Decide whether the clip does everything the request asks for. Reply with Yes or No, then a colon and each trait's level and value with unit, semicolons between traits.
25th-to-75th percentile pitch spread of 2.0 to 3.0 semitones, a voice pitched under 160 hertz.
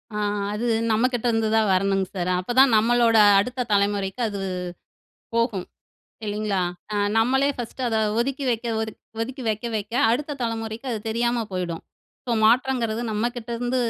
No: narrow, 2.6 semitones; high, 225 Hz